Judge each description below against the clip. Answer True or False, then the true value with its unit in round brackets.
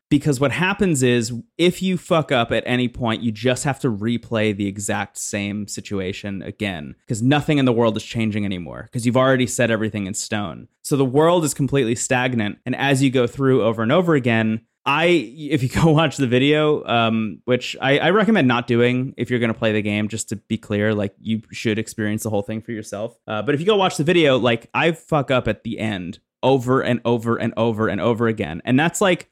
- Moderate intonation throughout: True (4.0 semitones)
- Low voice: True (120 Hz)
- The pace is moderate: False (225 wpm)